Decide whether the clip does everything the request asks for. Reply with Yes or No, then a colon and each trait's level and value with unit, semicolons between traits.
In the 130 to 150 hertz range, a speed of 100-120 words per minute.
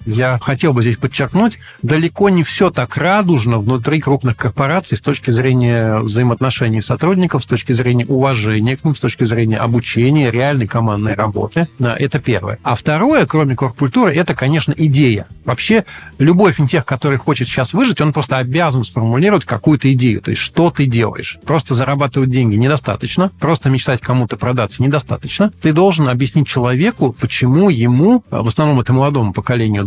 No: low, 135 Hz; fast, 160 wpm